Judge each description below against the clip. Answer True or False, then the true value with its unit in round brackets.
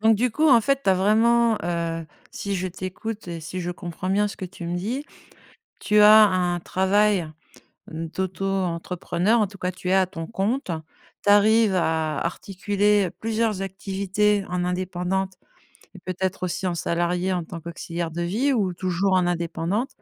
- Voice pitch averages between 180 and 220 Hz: True (185 Hz)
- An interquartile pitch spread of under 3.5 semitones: True (2.9 semitones)